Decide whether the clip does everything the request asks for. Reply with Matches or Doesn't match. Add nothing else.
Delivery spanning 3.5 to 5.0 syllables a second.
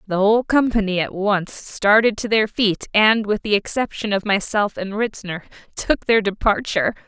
Matches